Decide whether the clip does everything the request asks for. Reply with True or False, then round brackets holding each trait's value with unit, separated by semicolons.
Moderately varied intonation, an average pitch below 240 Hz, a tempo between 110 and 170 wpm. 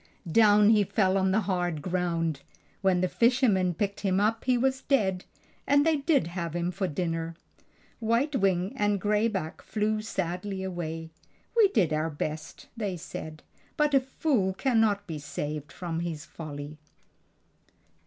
True (4.8 semitones; 190 Hz; 155 wpm)